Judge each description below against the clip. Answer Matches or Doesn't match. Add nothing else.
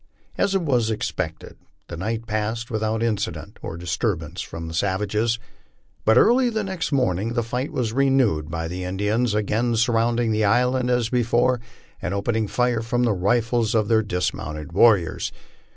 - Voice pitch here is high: Doesn't match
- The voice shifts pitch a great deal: Doesn't match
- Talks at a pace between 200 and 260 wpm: Doesn't match